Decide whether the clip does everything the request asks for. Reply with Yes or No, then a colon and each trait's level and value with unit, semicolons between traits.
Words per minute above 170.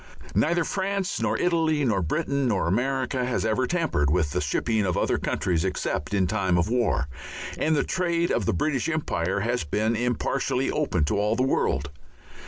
Yes: average, 180 wpm